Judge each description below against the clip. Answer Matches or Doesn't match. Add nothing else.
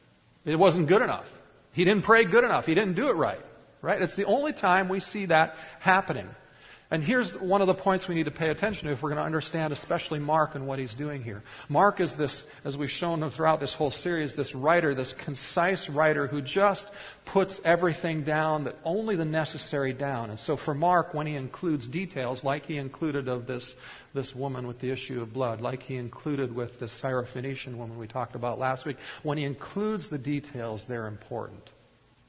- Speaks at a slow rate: Doesn't match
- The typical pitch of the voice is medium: Matches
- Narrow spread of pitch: Doesn't match